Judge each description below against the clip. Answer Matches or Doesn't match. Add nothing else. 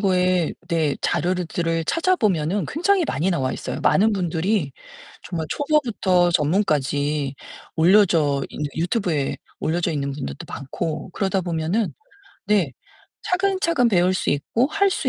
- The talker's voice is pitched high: Doesn't match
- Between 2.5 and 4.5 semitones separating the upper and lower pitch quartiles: Doesn't match